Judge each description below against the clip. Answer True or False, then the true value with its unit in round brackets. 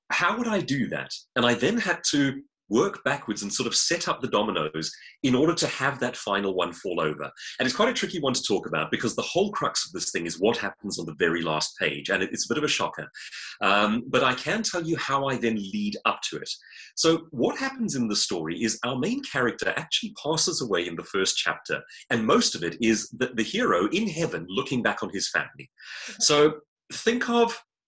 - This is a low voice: False (150 Hz)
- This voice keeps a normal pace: False (230 wpm)